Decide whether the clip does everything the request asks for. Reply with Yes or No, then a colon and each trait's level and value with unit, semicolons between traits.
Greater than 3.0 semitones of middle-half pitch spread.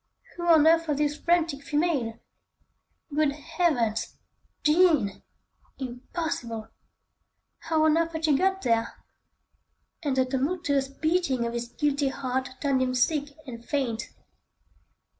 Yes: average, 4.1 semitones